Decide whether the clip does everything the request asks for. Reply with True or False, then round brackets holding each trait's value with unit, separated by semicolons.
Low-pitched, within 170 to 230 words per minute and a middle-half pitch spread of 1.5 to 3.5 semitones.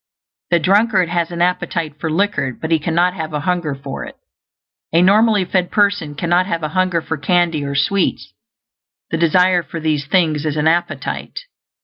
False (170 Hz; 175 wpm; 2.8 semitones)